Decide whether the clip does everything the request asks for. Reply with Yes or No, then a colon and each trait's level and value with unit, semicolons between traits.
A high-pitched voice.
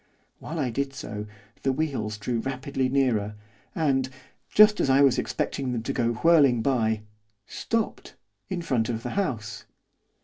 No: low, 130 Hz